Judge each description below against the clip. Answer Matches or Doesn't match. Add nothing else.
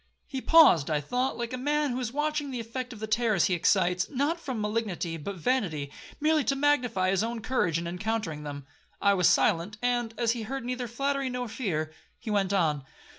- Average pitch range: Doesn't match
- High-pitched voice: Matches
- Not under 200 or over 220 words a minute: Matches